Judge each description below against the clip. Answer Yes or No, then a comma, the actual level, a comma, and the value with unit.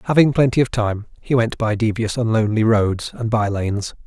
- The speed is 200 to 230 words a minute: Yes, fast, 205 wpm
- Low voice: Yes, low, 115 Hz